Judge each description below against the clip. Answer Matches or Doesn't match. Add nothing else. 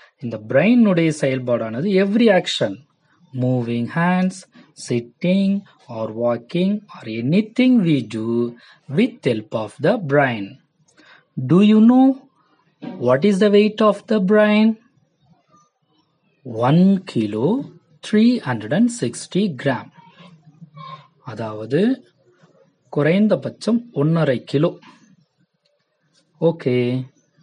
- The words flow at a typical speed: Matches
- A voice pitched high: Doesn't match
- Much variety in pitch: Matches